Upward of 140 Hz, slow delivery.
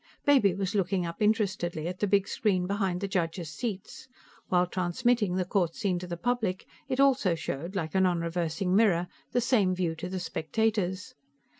No: medium, 185 Hz; average, 175 wpm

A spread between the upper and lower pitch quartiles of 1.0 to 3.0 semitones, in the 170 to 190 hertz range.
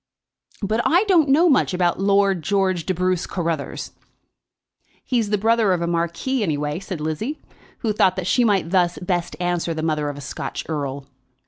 No: average, 4.2 semitones; medium, 185 Hz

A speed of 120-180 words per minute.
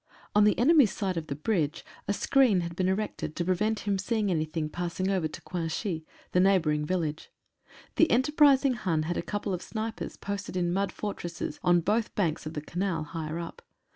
No: average, 195 wpm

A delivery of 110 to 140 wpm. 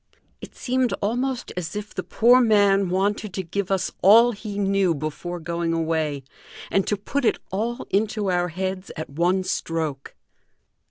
No: average, 160 wpm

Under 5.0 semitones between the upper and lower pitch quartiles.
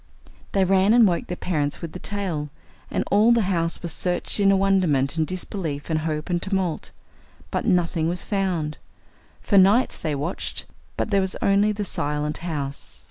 Yes: average, 3.8 semitones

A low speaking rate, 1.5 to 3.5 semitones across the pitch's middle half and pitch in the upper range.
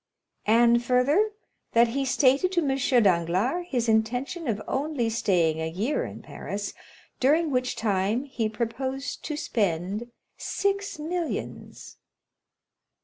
No: slow, 120 wpm; average, 4.9 semitones; high, 245 Hz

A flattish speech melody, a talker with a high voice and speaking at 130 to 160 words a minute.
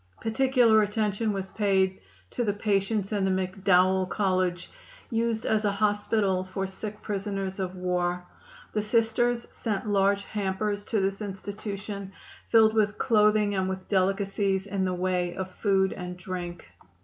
Yes: narrow, 2.0 semitones; high, 200 Hz; average, 145 wpm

